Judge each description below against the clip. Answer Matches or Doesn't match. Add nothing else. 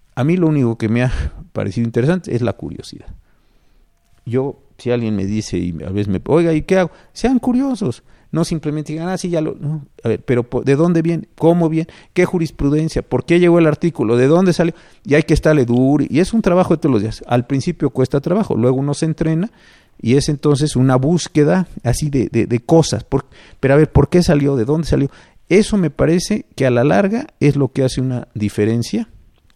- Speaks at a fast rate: Matches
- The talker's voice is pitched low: Doesn't match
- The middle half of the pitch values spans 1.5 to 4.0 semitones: Doesn't match